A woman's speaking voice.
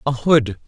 No: male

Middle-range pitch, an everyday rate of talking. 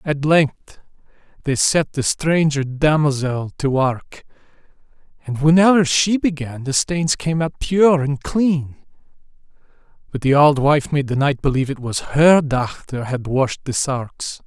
Yes: medium, 145 Hz; average, 150 wpm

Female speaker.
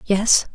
Yes: female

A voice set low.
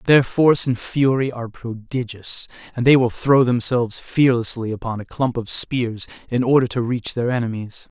Yes: low, 120 Hz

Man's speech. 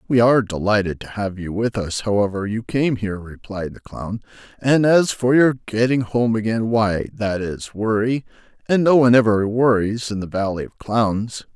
Yes: male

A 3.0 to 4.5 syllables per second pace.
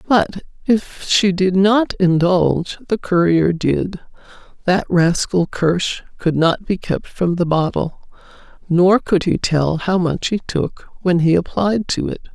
Yes: 3.8 syllables/s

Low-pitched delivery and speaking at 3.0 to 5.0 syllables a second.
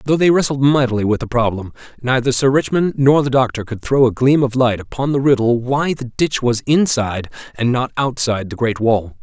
No: low, 125 Hz; 5.5 syllables/s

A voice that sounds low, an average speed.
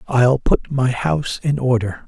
Yes: low, 130 Hz; average, 175 wpm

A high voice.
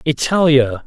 No: medium, 140 Hz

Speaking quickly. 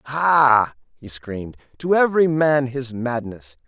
No: slow, 130 wpm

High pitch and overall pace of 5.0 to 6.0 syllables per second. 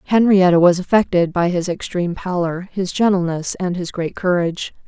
No: medium, 180 Hz; 5.3 syllables/s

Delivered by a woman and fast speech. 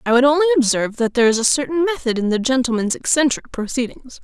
Yes: female; fast, 215 wpm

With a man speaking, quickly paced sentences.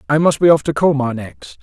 Yes: male; fast, 260 wpm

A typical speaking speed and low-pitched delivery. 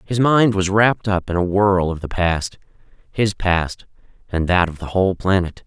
Yes: average, 190 wpm; very low, 95 Hz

